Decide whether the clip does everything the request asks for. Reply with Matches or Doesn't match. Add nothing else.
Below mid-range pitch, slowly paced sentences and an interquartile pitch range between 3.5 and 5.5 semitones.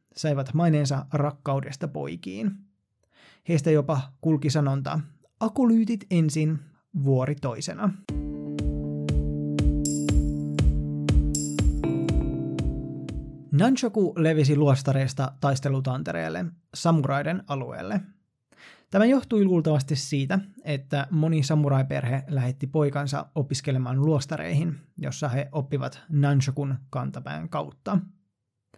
Doesn't match